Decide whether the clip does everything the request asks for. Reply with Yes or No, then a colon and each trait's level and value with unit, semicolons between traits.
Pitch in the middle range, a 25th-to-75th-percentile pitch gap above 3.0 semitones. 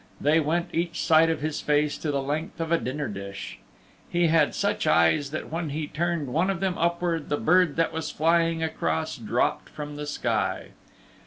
No: medium, 155 Hz; narrow, 2.4 semitones